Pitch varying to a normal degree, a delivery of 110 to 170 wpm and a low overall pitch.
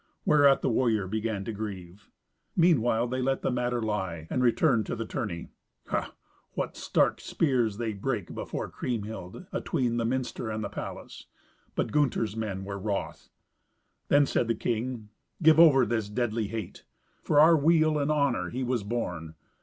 Yes: average, 3.9 semitones; average, 160 wpm; low, 115 Hz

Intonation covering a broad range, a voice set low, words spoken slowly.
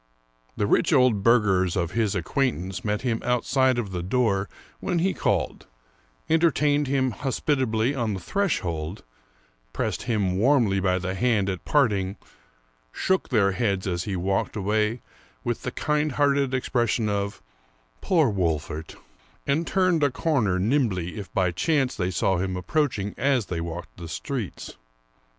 No: wide, 6.2 semitones; low, 110 Hz; average, 155 wpm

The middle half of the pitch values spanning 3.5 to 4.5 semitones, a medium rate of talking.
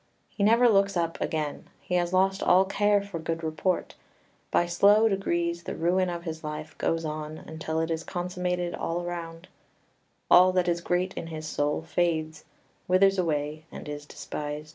No: average, 2.7 semitones; average, 170 wpm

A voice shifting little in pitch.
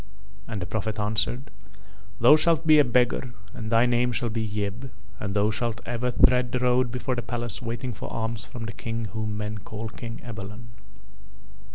Yes: narrow, 2.3 semitones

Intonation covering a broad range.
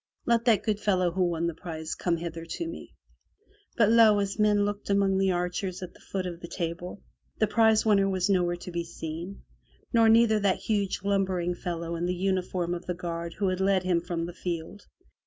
No: average, 2.8 semitones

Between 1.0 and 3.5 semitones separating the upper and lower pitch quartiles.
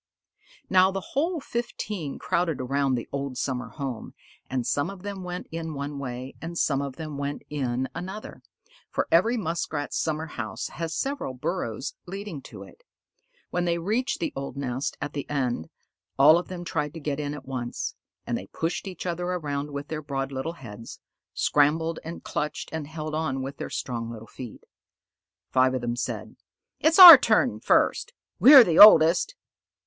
No: average, 4.6 semitones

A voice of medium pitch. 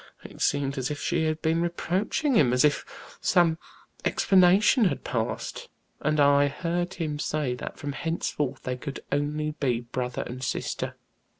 Yes: medium, 150 Hz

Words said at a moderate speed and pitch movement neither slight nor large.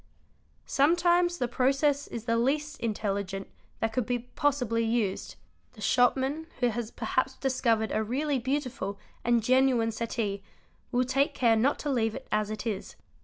Yes: average, 155 wpm; average, 3.4 semitones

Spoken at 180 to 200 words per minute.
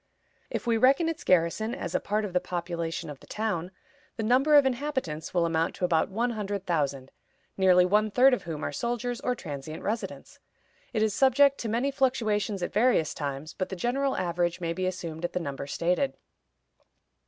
Yes: average, 190 wpm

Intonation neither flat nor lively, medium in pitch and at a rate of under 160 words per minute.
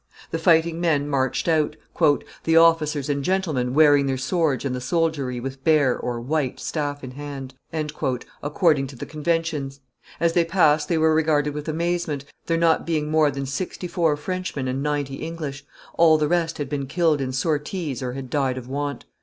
No: average, 3.2 semitones; medium, 150 Hz; average, 180 wpm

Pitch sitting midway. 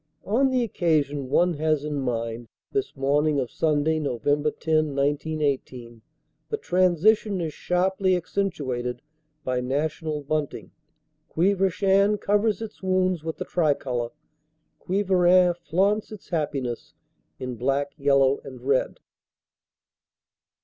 Yes: medium, 155 Hz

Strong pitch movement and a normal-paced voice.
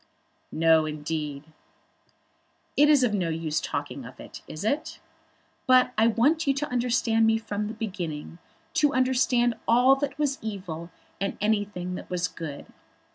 Yes: wide, 7.2 semitones; average, 155 wpm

